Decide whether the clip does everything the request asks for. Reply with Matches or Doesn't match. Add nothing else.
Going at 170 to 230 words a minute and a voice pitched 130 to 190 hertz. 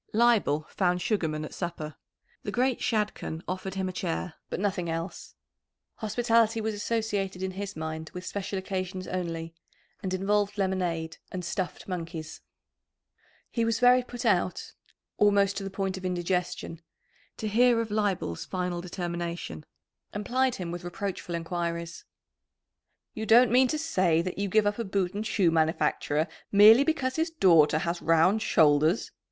Doesn't match